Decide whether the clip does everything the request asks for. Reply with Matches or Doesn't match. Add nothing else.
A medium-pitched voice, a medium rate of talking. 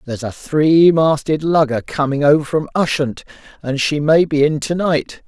Matches